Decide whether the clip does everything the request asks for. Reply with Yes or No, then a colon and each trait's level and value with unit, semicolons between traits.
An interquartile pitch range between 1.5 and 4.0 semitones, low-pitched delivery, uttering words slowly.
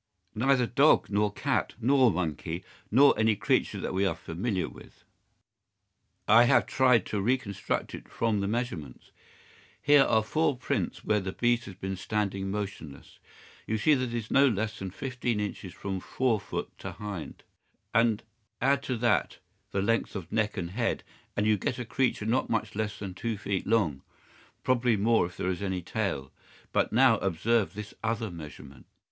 No: average, 3.7 semitones; low, 110 Hz; average, 170 wpm